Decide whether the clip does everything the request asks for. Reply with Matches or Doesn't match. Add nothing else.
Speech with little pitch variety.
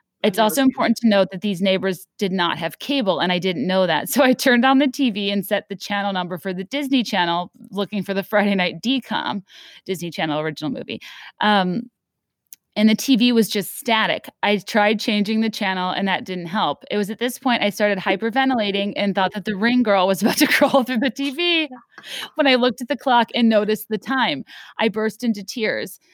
Doesn't match